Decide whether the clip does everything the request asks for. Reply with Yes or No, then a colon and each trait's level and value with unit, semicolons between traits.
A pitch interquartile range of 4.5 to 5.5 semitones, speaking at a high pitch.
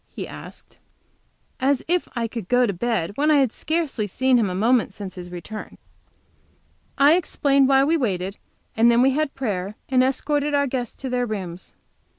Yes: average, 5.2 semitones; high, 245 Hz